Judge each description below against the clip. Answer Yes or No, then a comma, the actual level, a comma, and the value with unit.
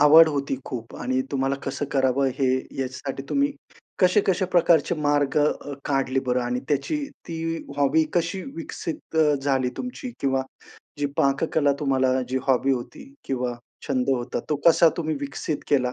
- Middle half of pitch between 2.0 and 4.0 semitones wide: Yes, average, 3.4 semitones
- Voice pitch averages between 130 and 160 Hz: Yes, medium, 140 Hz